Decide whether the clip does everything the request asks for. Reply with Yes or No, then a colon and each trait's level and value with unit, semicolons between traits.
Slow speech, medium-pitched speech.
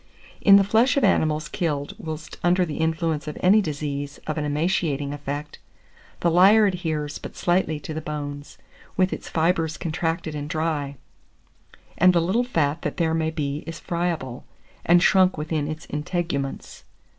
No: average, 160 wpm; medium, 160 Hz